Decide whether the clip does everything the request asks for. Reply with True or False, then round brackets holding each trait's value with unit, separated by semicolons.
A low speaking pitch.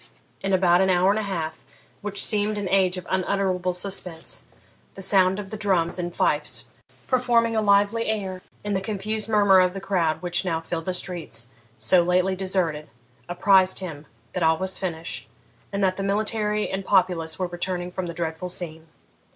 False (185 Hz)